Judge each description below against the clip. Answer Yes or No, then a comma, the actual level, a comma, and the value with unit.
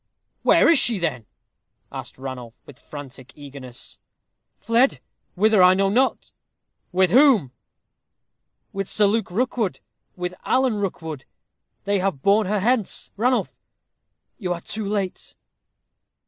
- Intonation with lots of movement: Yes, wide, 6.2 semitones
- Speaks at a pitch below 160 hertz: No, high, 195 Hz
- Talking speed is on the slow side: Yes, slow, 120 wpm